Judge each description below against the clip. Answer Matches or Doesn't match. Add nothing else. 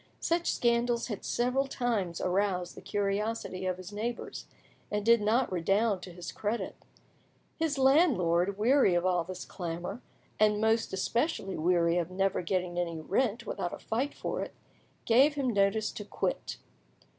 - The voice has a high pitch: Matches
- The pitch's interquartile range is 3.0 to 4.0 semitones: Doesn't match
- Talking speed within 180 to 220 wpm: Doesn't match